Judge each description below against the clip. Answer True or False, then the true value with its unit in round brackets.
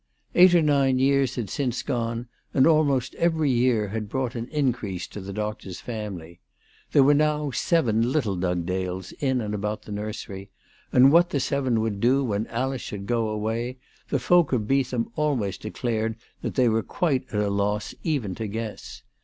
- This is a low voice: True (120 Hz)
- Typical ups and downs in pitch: True (4.5 semitones)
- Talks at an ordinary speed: True (180 wpm)